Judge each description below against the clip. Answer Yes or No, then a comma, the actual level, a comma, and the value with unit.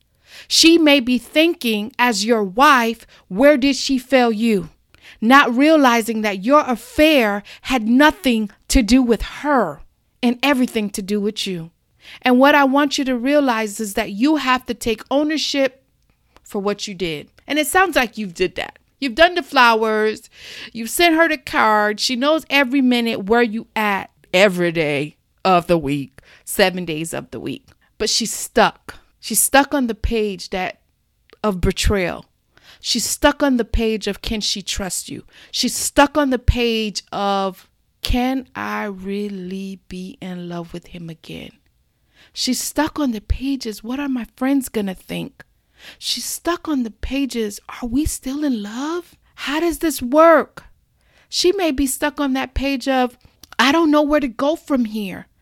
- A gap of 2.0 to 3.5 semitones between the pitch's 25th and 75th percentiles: No, average, 5.2 semitones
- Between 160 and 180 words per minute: Yes, average, 170 wpm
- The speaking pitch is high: Yes, high, 245 Hz